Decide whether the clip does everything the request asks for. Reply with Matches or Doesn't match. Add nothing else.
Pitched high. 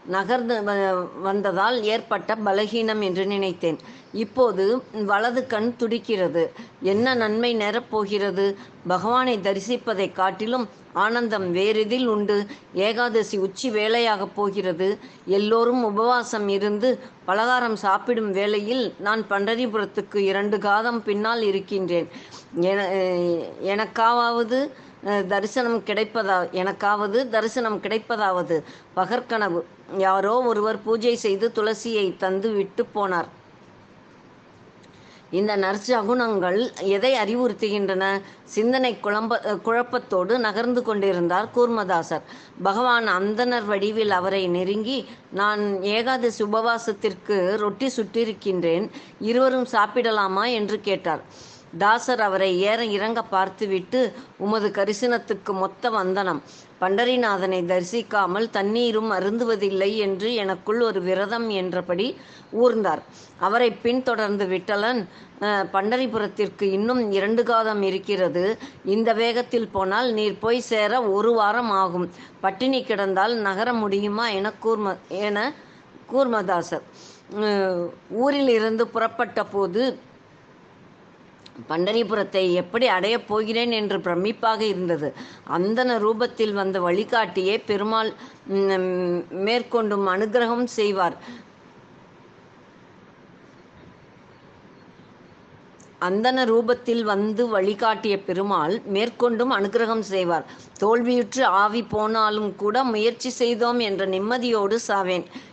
Matches